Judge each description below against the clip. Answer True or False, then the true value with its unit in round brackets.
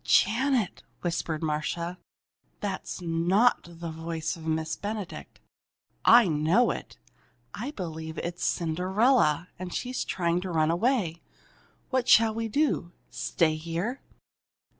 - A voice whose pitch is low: False (175 Hz)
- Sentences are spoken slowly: True (120 wpm)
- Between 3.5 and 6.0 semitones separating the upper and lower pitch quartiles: True (5.2 semitones)